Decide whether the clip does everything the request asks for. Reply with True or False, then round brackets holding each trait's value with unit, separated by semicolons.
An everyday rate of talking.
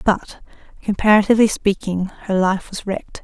False (130 wpm)